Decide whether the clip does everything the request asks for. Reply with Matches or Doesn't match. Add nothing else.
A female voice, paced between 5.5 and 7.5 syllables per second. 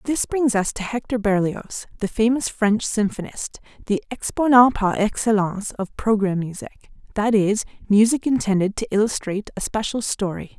Doesn't match